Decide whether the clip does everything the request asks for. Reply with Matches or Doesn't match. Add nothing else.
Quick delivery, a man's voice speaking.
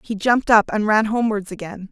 Doesn't match